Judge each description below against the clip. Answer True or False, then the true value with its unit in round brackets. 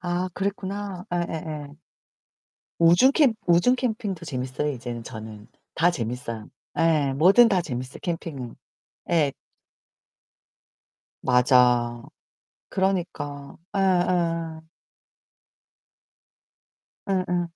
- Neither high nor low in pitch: True (165 Hz)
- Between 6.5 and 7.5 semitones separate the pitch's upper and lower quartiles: False (6.1 semitones)